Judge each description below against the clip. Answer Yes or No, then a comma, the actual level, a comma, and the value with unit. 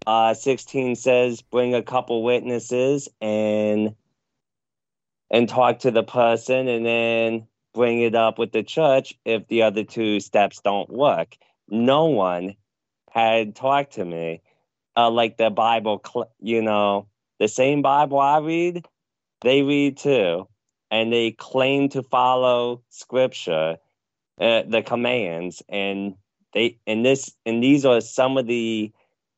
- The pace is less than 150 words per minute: Yes, slow, 135 wpm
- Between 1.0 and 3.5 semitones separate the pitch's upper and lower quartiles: Yes, average, 2.9 semitones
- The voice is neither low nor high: No, low, 115 Hz